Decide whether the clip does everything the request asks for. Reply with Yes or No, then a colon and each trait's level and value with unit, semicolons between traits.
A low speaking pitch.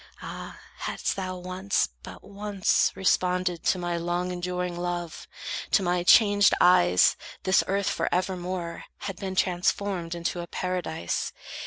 No: medium, 180 Hz